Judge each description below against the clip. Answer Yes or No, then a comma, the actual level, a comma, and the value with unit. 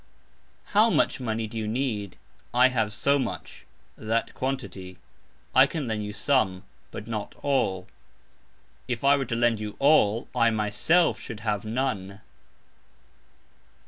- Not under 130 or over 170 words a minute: Yes, average, 140 wpm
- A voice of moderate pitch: No, low, 115 Hz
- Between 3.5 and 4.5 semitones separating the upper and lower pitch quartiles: Yes, average, 4.1 semitones